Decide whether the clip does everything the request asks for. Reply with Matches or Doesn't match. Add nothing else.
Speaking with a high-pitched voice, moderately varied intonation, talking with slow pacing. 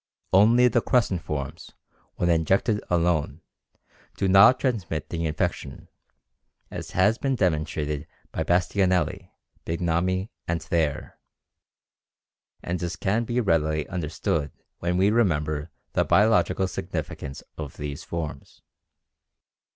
Doesn't match